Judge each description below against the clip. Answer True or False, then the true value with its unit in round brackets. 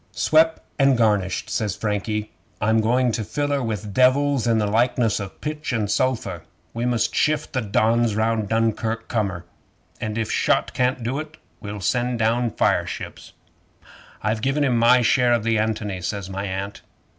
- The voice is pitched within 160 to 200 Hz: False (115 Hz)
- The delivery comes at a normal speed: True (170 wpm)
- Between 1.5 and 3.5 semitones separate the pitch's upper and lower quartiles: True (3.0 semitones)